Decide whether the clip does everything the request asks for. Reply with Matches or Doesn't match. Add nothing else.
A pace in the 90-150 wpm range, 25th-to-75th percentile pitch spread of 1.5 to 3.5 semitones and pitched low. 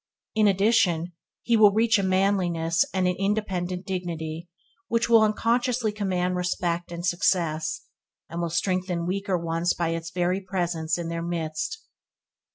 Doesn't match